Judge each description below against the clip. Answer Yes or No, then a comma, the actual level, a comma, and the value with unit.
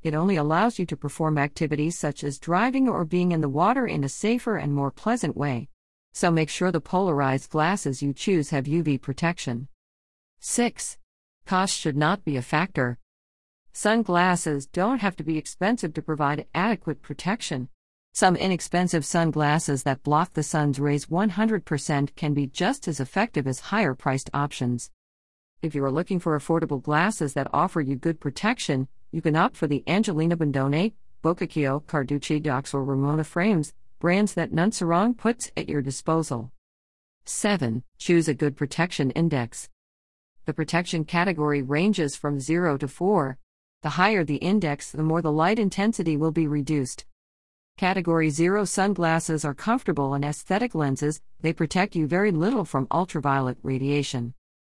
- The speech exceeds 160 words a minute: No, average, 155 wpm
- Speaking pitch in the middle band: Yes, medium, 155 Hz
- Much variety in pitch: No, average, 4.3 semitones